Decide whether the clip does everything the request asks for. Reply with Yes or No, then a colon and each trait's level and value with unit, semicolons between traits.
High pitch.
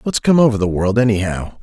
No: low, 105 Hz